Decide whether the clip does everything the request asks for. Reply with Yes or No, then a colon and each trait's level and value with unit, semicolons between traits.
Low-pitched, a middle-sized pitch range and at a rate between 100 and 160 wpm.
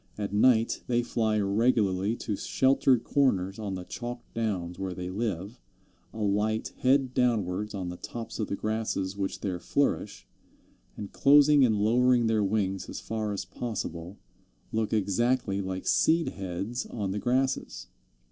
Yes: low, 110 Hz; average, 3.8 semitones; average, 145 wpm